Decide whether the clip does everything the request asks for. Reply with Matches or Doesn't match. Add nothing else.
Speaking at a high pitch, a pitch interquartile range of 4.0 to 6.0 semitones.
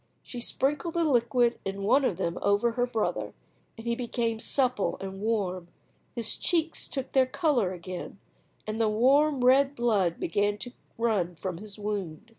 Matches